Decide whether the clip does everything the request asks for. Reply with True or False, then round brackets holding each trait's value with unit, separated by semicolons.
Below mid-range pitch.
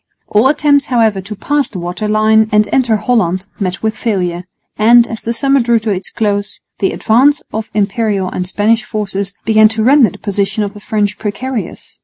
False (215 Hz)